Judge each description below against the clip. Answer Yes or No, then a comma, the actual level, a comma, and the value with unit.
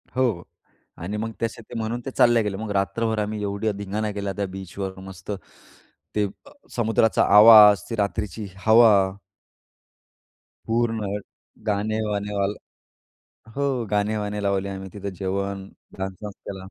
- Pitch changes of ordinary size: No, narrow, 2.0 semitones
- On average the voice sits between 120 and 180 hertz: No, low, 105 Hz